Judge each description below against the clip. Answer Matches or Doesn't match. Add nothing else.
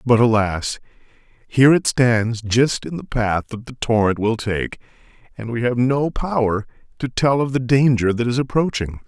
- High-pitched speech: Doesn't match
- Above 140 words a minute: Matches